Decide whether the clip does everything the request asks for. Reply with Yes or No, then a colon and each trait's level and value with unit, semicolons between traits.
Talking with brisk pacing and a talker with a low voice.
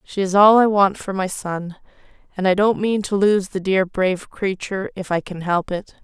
No: fast, 230 wpm; high, 190 Hz